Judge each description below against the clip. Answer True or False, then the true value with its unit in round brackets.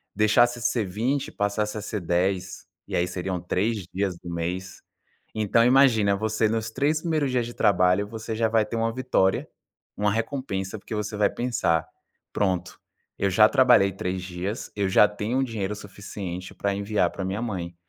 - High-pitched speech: False (105 Hz)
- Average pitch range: True (3.2 semitones)